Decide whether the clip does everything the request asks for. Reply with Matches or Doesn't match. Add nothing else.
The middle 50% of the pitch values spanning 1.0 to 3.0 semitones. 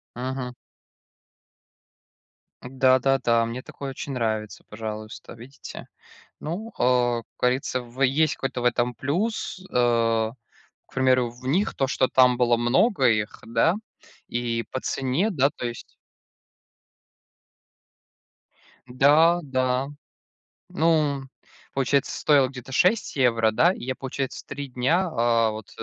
Matches